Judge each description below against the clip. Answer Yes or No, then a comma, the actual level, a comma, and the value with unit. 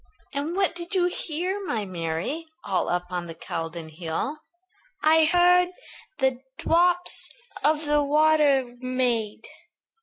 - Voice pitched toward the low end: No, very high, 290 Hz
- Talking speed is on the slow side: Yes, slow, 125 wpm